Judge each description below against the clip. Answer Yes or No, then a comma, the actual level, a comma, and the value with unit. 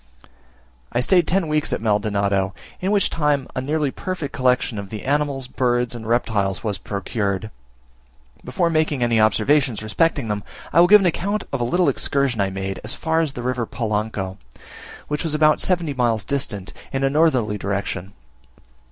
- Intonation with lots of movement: Yes, wide, 6.4 semitones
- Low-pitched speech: Yes, low, 125 Hz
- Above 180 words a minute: No, average, 170 wpm